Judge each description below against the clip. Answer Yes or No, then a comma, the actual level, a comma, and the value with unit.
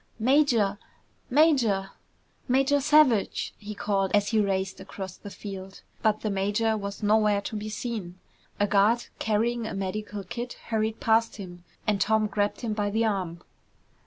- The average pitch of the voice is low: No, high, 210 Hz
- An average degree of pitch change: No, narrow, 2.3 semitones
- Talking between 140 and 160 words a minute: Yes, average, 155 wpm